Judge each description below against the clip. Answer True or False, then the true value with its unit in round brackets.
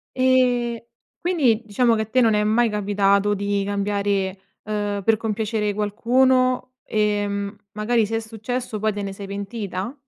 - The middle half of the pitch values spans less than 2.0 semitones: False (2.7 semitones)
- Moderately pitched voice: False (215 Hz)